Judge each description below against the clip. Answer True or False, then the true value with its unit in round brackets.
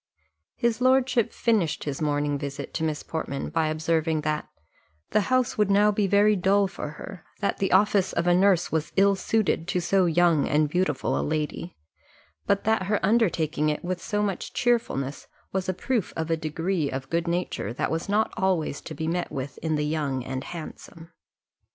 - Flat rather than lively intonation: False (4.6 semitones)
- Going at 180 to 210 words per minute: True (190 wpm)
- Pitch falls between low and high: True (170 Hz)